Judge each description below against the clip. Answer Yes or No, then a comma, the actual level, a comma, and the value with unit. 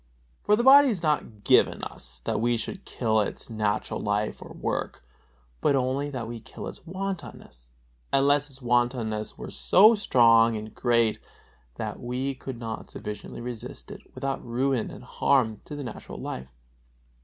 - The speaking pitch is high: No, low, 120 Hz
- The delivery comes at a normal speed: Yes, average, 160 wpm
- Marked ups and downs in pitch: No, average, 4.2 semitones